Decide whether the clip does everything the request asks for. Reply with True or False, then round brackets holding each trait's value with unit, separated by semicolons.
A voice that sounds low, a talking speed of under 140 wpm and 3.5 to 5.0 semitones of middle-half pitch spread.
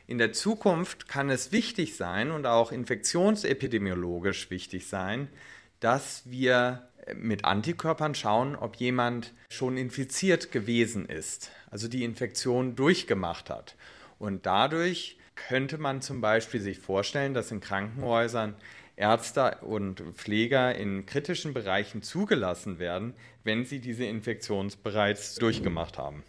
True (120 Hz; 125 wpm; 4.4 semitones)